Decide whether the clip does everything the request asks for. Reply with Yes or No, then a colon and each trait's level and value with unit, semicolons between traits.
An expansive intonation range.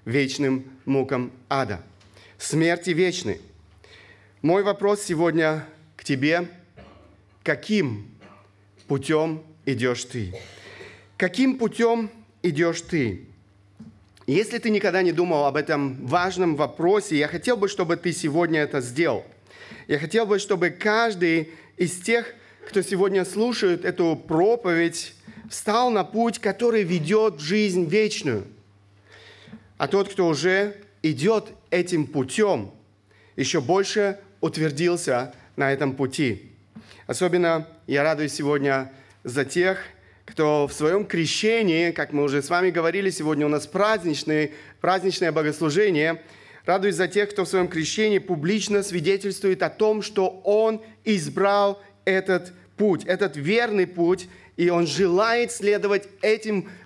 Yes: wide, 5.9 semitones